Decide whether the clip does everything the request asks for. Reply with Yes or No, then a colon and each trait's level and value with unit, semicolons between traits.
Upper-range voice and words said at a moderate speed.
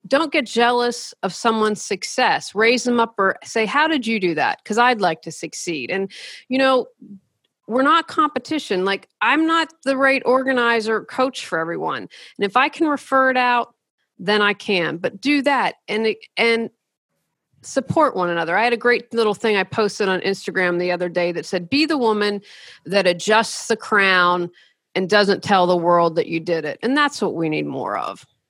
Yes: high, 220 Hz; average, 195 wpm